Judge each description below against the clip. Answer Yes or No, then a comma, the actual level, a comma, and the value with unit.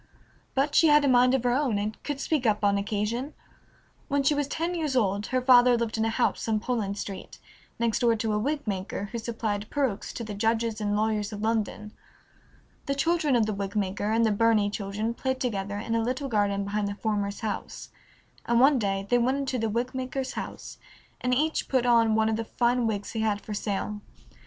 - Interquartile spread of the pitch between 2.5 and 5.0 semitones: Yes, average, 3.5 semitones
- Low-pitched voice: No, high, 225 Hz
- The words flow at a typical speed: No, fast, 215 wpm